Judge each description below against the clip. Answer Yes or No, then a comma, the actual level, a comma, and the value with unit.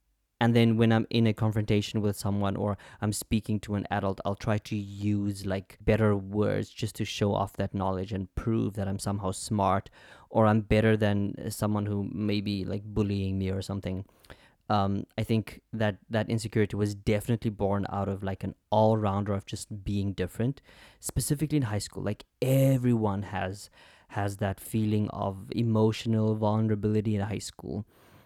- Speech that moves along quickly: No, average, 170 wpm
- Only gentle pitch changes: Yes, narrow, 1.8 semitones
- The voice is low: Yes, low, 105 Hz